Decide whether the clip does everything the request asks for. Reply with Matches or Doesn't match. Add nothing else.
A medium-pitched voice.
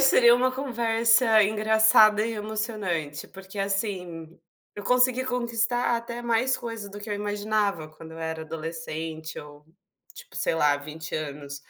Doesn't match